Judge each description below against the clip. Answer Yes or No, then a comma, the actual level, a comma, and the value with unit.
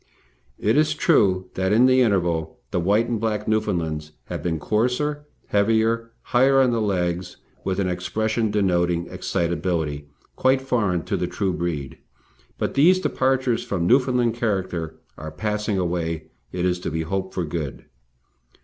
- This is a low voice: Yes, low, 100 Hz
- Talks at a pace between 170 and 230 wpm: No, average, 150 wpm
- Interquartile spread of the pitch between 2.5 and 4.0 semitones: No, average, 5.1 semitones